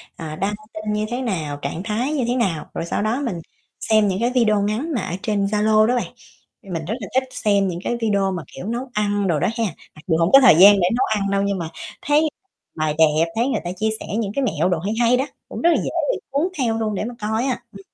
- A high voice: Yes, high, 210 Hz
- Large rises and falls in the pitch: No, average, 4.4 semitones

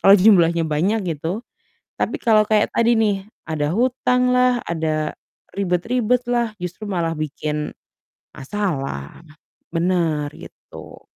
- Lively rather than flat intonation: Yes, wide, 5.8 semitones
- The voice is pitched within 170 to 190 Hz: Yes, medium, 185 Hz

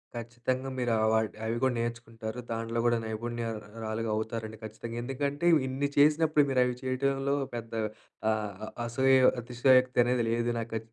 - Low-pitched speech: Yes, low, 120 Hz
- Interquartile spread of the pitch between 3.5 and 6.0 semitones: No, narrow, 2.5 semitones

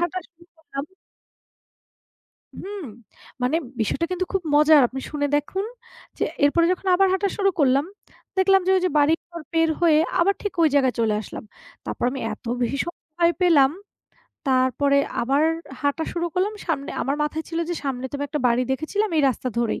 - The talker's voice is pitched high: Yes, very high, 310 Hz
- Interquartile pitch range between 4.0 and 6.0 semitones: Yes, average, 4.3 semitones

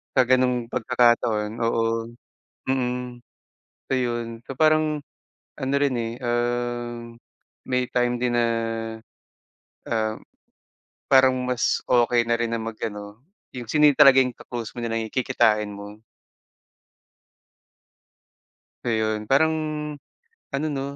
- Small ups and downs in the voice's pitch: Yes, narrow, 1.9 semitones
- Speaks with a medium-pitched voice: No, low, 120 Hz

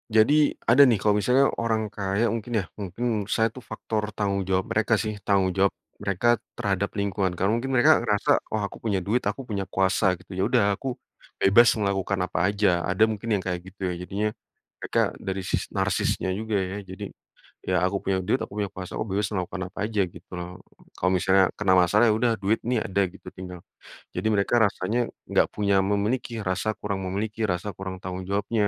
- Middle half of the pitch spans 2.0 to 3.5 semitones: Yes, narrow, 2.6 semitones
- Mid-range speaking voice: No, low, 100 Hz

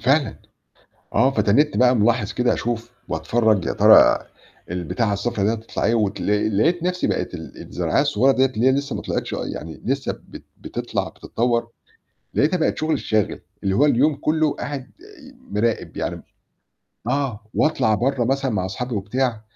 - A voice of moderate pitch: No, low, 120 Hz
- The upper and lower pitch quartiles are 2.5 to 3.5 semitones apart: No, average, 4.3 semitones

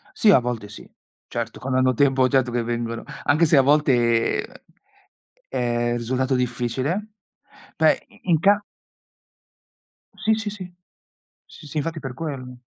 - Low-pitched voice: Yes, low, 130 Hz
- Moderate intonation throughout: Yes, average, 4.2 semitones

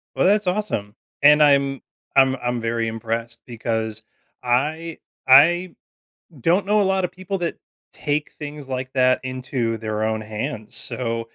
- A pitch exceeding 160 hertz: No, low, 130 Hz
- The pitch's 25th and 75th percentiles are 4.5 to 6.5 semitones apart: Yes, wide, 5.6 semitones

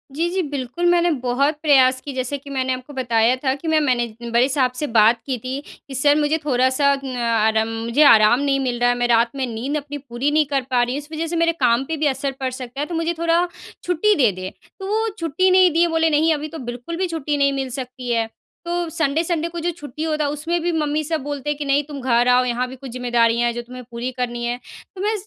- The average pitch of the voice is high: Yes, very high, 275 Hz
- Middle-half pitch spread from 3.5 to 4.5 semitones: Yes, average, 4.1 semitones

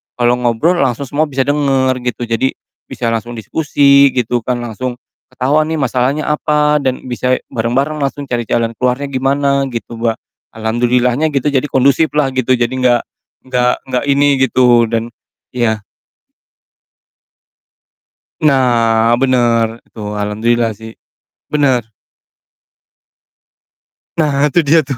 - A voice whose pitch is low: Yes, low, 125 Hz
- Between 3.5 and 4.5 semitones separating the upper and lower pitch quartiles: No, average, 2.8 semitones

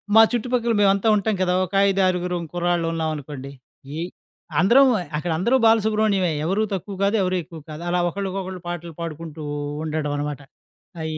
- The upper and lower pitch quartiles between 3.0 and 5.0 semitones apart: Yes, average, 3.7 semitones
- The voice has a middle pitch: Yes, medium, 180 Hz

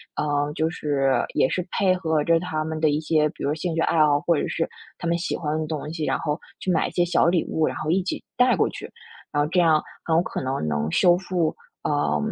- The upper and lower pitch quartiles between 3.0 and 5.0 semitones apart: No, narrow, 2.5 semitones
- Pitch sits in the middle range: Yes, medium, 160 Hz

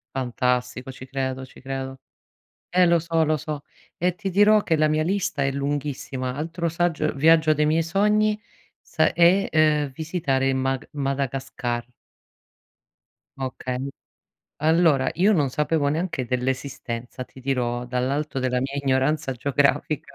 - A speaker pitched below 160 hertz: Yes, medium, 140 Hz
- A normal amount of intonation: Yes, average, 3.6 semitones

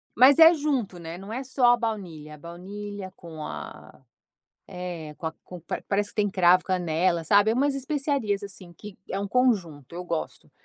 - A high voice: Yes, high, 195 Hz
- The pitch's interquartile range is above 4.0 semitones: Yes, average, 5.2 semitones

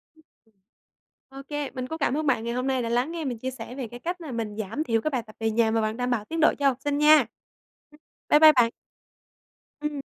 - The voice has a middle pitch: No, very high, 260 Hz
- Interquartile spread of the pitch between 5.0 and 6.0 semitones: No, average, 4.4 semitones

